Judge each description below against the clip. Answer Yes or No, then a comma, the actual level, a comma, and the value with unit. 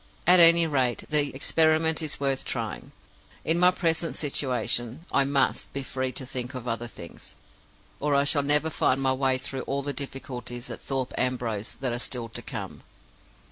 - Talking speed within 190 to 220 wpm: No, average, 180 wpm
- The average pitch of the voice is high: No, low, 135 Hz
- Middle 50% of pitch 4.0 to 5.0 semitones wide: No, average, 3.0 semitones